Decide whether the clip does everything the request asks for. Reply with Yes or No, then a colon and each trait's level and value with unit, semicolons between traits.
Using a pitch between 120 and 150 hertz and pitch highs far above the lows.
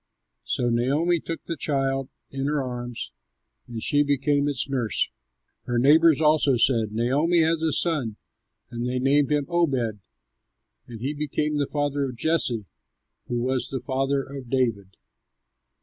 No: low, 135 Hz; average, 3.4 semitones